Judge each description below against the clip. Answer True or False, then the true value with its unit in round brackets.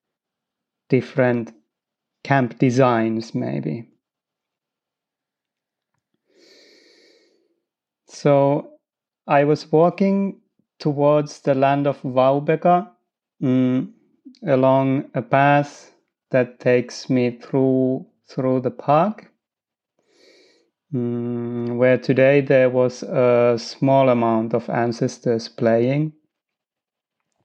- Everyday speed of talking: False (75 wpm)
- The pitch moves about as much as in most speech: False (7.2 semitones)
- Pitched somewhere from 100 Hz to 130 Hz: False (140 Hz)